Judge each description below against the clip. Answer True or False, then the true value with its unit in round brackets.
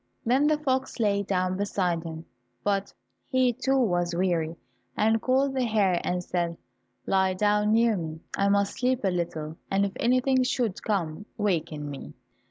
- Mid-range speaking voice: False (200 Hz)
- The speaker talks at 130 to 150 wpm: False (165 wpm)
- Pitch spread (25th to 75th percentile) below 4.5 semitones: False (5.2 semitones)